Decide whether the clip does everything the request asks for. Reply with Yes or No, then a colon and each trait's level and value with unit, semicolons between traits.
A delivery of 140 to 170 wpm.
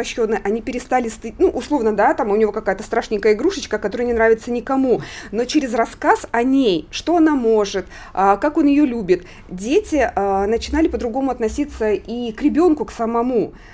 Yes: fast, 160 wpm